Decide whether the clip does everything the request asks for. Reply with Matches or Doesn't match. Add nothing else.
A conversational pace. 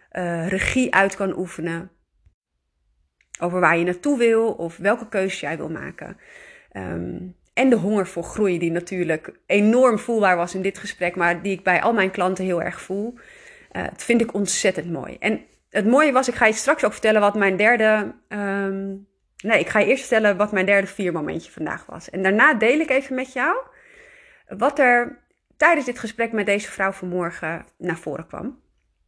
Matches